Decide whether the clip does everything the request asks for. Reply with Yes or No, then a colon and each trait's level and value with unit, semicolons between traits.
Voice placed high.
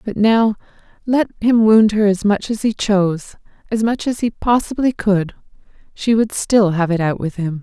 Yes: high, 205 Hz